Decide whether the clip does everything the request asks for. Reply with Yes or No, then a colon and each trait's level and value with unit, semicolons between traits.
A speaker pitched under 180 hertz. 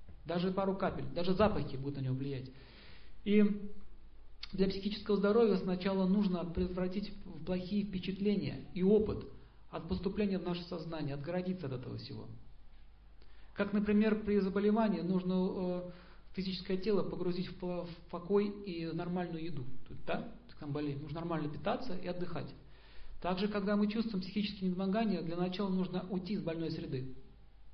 No: medium, 185 Hz